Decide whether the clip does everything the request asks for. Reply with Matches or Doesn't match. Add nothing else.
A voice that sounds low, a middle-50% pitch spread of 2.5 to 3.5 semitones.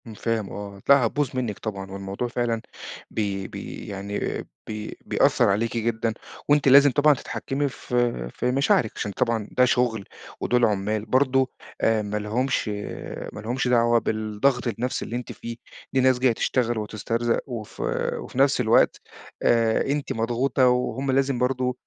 Matches